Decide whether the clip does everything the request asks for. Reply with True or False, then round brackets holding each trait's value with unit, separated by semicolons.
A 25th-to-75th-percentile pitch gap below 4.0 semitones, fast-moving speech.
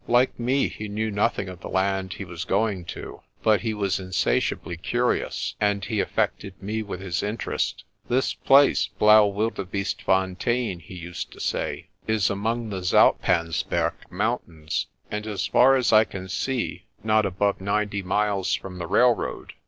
False (2.8 semitones; 155 wpm)